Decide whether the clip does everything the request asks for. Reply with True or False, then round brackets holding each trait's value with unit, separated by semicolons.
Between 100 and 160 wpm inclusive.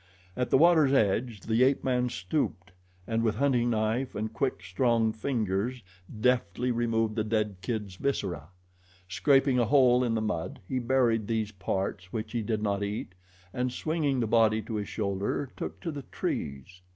False (170 wpm)